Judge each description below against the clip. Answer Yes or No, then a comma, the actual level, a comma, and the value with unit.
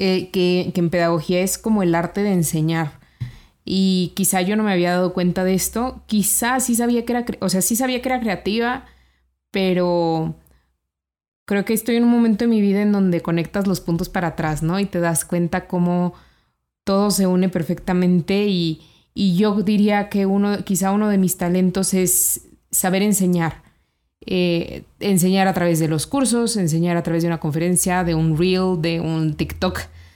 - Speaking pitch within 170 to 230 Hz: Yes, medium, 185 Hz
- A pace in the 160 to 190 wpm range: Yes, average, 185 wpm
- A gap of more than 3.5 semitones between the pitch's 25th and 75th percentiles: No, average, 3.0 semitones